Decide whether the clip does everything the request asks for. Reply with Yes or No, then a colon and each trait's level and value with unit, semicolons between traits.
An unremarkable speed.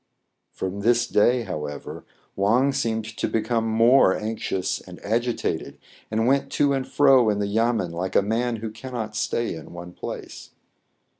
Yes: average, 160 wpm